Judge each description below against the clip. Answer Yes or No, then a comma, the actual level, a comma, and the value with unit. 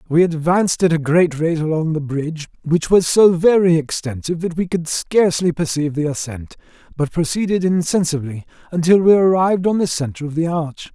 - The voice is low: No, medium, 165 Hz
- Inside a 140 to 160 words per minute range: No, average, 180 wpm